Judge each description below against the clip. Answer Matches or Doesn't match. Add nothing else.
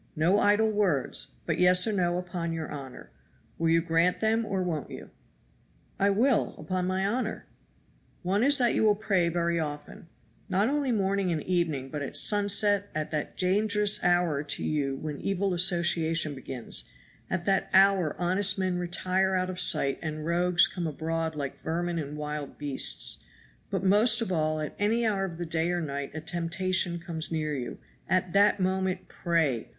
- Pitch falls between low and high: Matches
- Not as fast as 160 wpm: Doesn't match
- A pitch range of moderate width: Matches